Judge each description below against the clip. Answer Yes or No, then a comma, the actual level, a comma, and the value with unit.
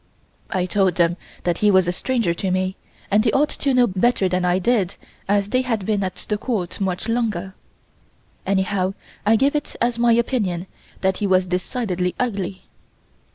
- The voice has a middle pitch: No, high, 195 Hz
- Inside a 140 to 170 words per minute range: No, average, 180 wpm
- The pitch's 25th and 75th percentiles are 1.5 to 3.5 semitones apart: No, average, 4.0 semitones